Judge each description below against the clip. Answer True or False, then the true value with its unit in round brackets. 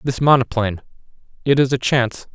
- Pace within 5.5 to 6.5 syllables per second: True (6.2 syllables/s)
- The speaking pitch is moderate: False (125 Hz)